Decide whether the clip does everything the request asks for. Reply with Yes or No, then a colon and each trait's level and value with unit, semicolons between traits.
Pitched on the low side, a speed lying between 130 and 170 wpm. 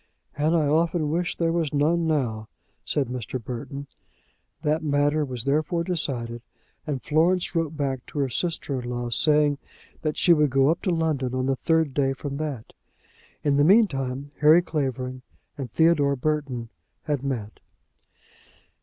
No: medium, 145 Hz; average, 155 wpm